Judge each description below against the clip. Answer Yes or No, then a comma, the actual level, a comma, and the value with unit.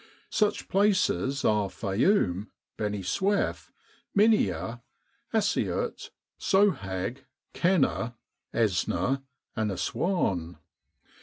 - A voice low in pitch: Yes, low, 120 Hz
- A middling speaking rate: No, slow, 70 wpm